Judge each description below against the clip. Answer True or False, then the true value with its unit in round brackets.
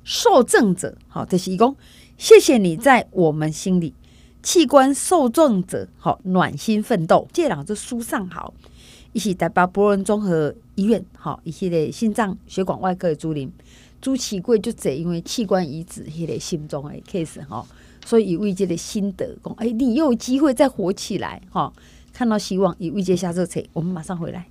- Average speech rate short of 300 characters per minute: True (280 characters per minute)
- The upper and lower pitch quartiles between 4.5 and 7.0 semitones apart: True (5.3 semitones)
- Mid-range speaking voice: False (195 Hz)